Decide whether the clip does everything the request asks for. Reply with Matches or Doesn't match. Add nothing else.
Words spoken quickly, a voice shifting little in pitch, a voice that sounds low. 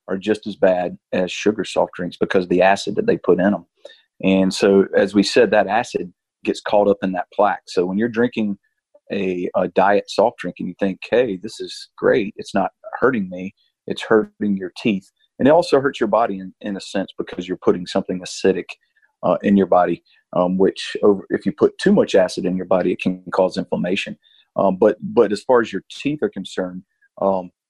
Matches